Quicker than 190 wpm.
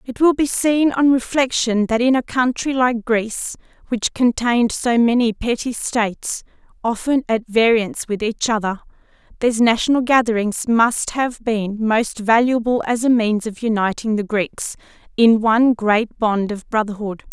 No: average, 155 wpm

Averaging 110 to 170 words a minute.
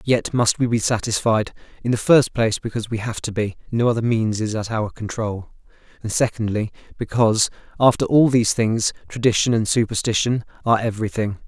Yes: average, 150 wpm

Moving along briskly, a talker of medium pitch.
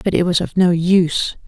Yes: fast, 245 wpm; medium, 175 Hz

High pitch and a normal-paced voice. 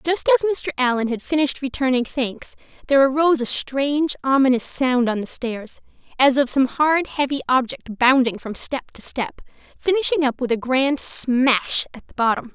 Yes: very high, 265 Hz; average, 175 wpm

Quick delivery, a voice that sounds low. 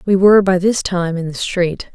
No: fast, 245 wpm; medium, 185 Hz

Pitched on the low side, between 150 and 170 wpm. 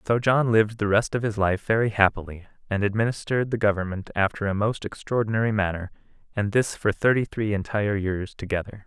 No: low, 105 Hz; average, 185 wpm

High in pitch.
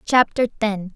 Yes: high, 215 Hz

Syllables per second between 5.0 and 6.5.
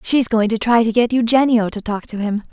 Yes: 5.5 syllables/s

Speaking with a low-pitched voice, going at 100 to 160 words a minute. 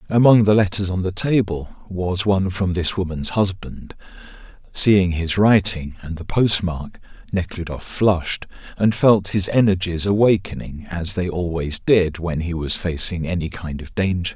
Yes: very low, 90 Hz; average, 155 wpm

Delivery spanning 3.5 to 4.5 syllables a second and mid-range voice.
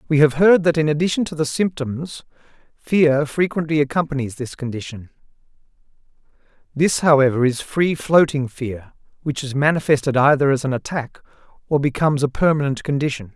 No: 5.5 syllables/s; medium, 145 Hz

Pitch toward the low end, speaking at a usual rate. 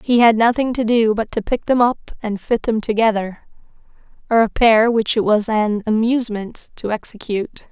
No: high, 225 Hz; average, 170 wpm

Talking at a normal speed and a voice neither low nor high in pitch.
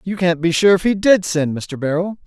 No: fast, 265 wpm; medium, 175 Hz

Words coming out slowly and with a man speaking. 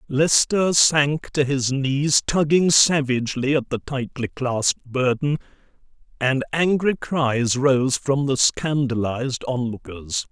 Yes: slow, 115 wpm; male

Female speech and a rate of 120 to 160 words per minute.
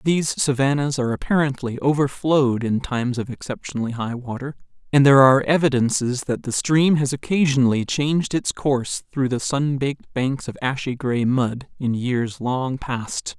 No: male; average, 155 wpm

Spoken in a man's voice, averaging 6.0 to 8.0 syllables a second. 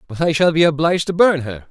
Yes: male; 6.5 syllables/s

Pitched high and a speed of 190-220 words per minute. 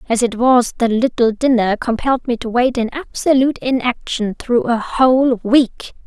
No: high, 245 Hz; average, 170 wpm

